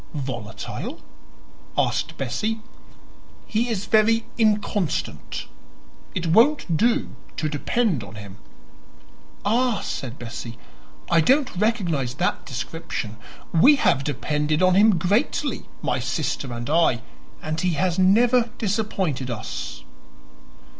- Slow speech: Yes, slow, 110 wpm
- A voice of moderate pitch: Yes, medium, 175 Hz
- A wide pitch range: Yes, wide, 8.5 semitones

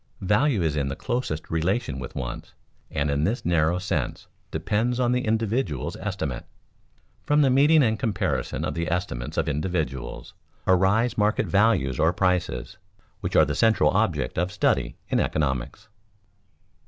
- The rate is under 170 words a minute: Yes, average, 150 wpm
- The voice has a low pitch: Yes, very low, 95 Hz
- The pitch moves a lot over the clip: Yes, wide, 6.5 semitones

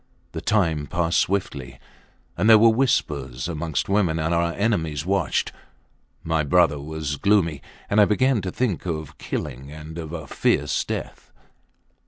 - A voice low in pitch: Yes, very low, 85 Hz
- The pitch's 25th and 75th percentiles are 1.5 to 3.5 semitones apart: No, average, 4.8 semitones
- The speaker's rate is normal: Yes, average, 150 wpm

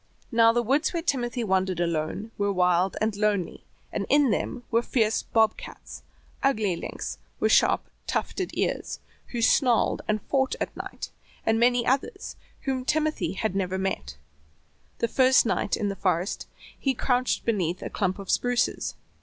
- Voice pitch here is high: Yes, high, 225 Hz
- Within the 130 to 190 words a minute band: Yes, average, 160 wpm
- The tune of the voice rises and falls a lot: No, average, 4.8 semitones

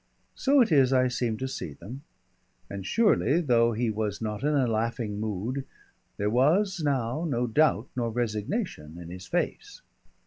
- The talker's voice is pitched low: Yes, low, 120 Hz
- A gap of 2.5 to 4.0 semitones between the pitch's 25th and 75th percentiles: No, average, 4.8 semitones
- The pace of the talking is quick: No, average, 165 wpm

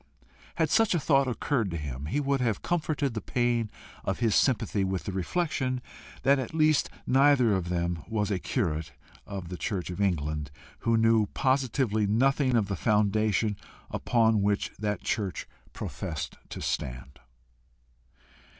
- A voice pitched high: No, low, 110 Hz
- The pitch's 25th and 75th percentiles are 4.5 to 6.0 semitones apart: Yes, wide, 5.6 semitones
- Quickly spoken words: No, average, 150 wpm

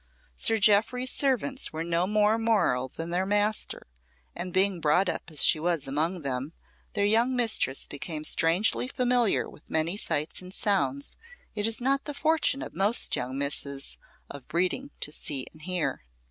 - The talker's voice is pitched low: No, medium, 185 Hz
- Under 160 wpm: No, average, 165 wpm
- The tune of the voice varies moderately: No, wide, 6.5 semitones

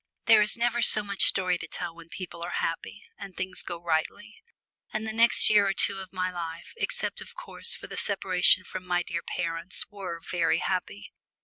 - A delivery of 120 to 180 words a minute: No, average, 200 wpm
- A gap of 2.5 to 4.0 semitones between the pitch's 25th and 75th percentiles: Yes, average, 3.5 semitones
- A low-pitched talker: No, medium, 185 Hz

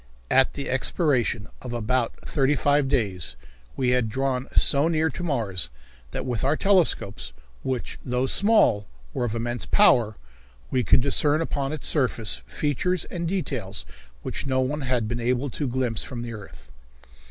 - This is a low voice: Yes, low, 130 Hz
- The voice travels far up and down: No, average, 3.7 semitones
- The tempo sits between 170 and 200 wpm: No, average, 160 wpm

